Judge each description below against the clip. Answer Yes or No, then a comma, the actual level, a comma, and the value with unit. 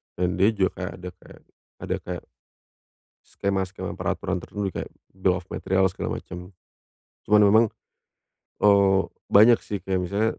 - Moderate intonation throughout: No, narrow, 1.8 semitones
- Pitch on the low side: Yes, very low, 95 Hz